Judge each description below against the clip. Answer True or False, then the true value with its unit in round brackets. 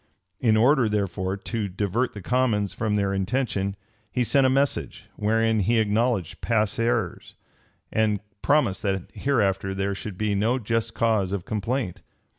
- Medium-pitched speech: False (110 Hz)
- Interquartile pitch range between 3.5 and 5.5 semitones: False (3.1 semitones)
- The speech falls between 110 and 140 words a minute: False (150 wpm)